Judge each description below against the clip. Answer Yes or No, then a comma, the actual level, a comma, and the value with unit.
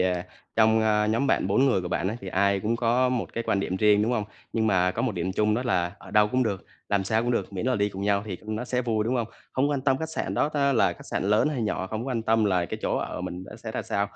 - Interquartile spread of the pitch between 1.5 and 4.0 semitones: Yes, average, 3.6 semitones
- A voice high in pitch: No, low, 110 Hz